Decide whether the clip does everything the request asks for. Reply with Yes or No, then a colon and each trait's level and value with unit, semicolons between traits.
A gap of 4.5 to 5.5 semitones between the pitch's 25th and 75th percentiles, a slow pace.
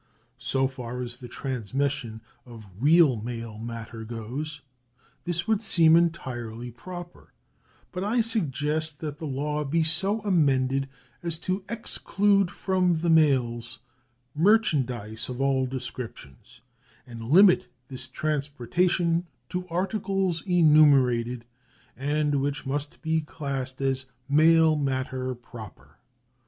Yes: average, 5.1 semitones; slow, 115 wpm